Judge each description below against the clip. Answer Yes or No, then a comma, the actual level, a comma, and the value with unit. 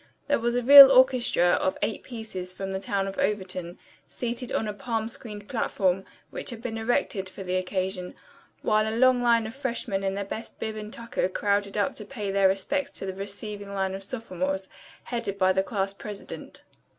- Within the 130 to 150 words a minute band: No, average, 195 wpm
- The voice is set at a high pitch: Yes, high, 205 Hz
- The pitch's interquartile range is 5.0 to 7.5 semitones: No, average, 3.4 semitones